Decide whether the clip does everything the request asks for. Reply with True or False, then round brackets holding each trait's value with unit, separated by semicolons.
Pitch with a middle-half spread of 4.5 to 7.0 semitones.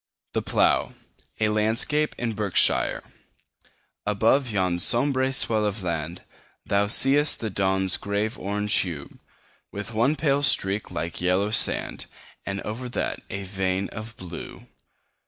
False (3.4 semitones)